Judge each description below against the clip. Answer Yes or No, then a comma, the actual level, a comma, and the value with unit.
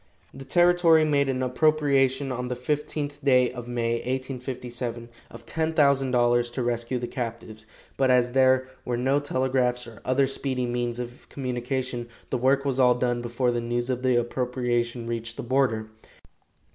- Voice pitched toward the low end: Yes, low, 125 Hz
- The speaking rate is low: No, average, 160 wpm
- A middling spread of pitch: No, narrow, 2.0 semitones